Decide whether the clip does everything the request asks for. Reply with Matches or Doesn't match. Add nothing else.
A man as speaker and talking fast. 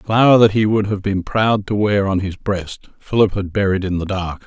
Matches